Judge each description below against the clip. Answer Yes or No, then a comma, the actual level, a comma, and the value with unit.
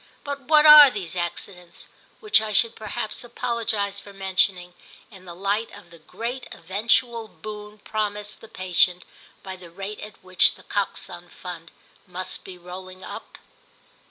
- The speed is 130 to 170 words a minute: Yes, average, 150 wpm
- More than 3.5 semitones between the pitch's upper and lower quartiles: No, average, 3.2 semitones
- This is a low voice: No, high, 200 Hz